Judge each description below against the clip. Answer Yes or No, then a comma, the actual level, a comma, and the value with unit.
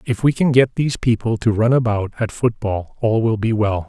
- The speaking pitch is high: No, low, 115 Hz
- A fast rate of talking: Yes, fast, 230 wpm